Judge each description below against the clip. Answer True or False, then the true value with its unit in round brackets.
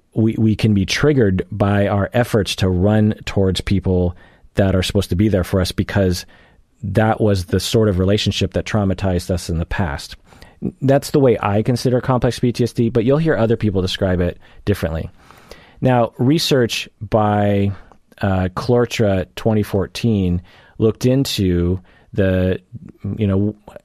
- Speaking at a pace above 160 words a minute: False (150 wpm)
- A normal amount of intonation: True (3.4 semitones)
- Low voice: True (100 Hz)